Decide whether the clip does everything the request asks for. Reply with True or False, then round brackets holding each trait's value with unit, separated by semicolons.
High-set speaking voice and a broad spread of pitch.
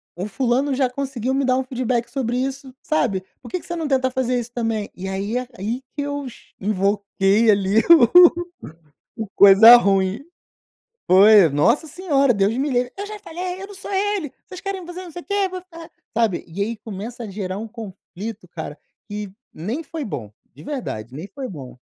True (240 Hz; 6.2 semitones)